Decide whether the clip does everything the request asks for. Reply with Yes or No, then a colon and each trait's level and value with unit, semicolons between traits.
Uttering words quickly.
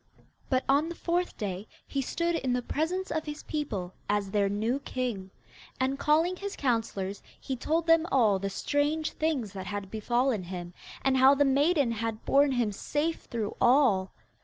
No: average, 175 wpm